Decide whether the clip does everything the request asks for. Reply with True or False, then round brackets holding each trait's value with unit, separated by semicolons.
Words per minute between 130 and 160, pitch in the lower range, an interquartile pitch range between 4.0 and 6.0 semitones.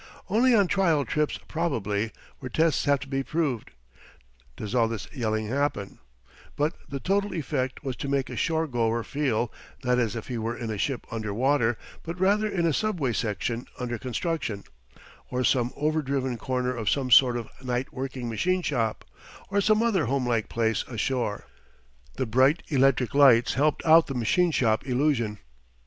False (170 wpm; 130 Hz; 4.8 semitones)